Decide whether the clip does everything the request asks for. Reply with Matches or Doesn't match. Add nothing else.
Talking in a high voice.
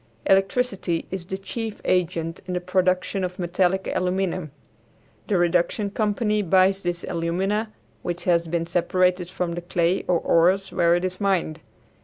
Doesn't match